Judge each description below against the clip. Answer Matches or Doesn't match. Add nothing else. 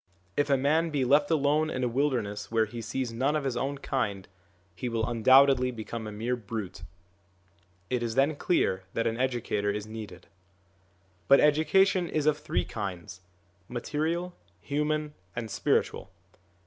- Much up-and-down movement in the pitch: Doesn't match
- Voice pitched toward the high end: Doesn't match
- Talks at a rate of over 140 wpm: Matches